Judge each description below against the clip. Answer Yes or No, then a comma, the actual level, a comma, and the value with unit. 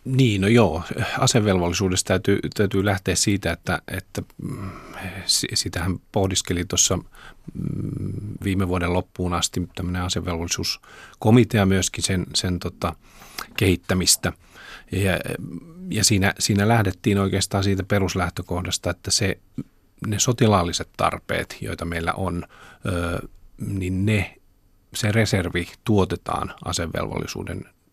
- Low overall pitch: Yes, very low, 95 Hz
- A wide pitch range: No, average, 2.9 semitones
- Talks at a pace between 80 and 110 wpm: Yes, average, 100 wpm